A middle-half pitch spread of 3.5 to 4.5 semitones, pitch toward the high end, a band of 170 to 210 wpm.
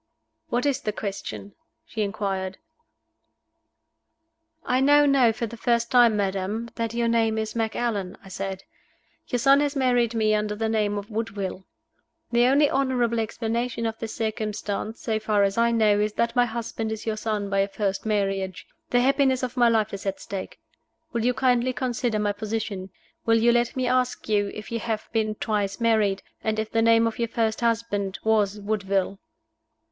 No: narrow, 2.4 semitones; high, 220 Hz; average, 180 wpm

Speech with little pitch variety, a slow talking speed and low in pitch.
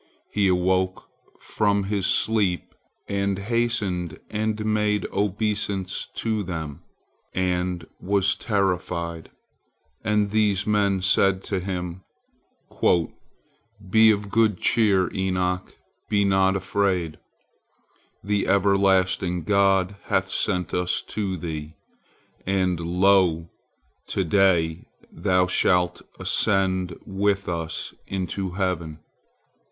Yes: narrow, 2.1 semitones; slow, 95 wpm; very low, 95 Hz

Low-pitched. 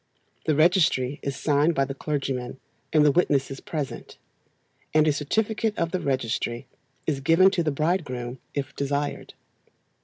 No: medium, 145 Hz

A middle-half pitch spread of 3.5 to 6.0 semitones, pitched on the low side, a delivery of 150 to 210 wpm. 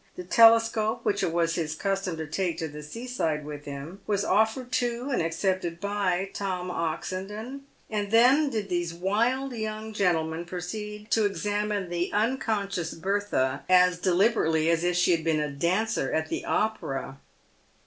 No: average, 4.5 semitones; high, 190 Hz; average, 165 wpm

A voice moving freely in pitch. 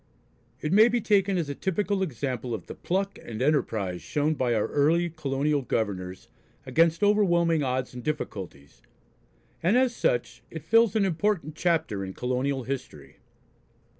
Yes: wide, 7.2 semitones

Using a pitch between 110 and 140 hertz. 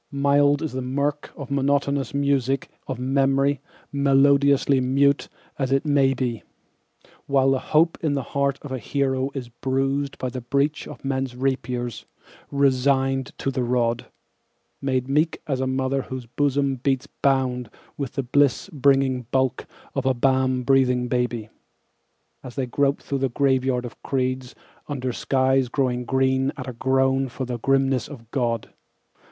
Yes: low, 135 Hz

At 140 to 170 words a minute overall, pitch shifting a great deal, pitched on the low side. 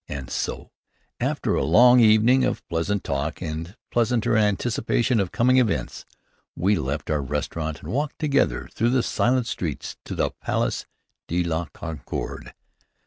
Yes: average, 145 wpm; wide, 7.3 semitones; low, 100 Hz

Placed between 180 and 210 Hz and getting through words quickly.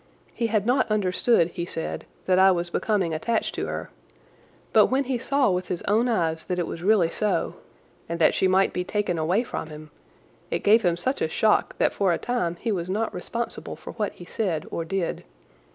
Yes: high, 190 Hz; fast, 210 wpm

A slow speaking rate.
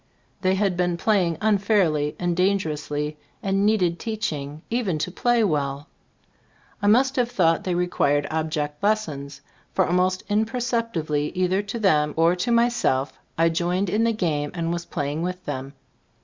No: average, 155 wpm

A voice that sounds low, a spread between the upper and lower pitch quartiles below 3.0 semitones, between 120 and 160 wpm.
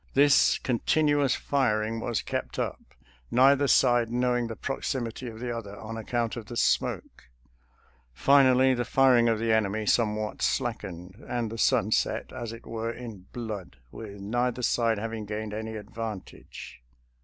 Yes: low, 115 Hz; narrow, 2.4 semitones; average, 155 wpm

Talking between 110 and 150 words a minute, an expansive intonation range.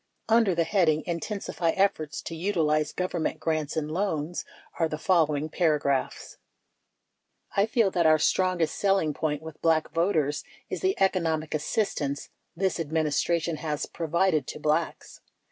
No: average, 145 wpm; average, 3.2 semitones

